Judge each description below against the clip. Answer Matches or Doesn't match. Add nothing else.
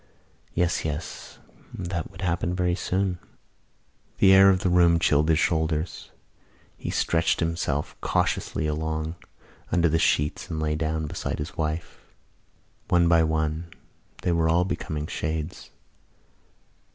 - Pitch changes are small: Matches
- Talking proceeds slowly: Matches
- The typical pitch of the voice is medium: Doesn't match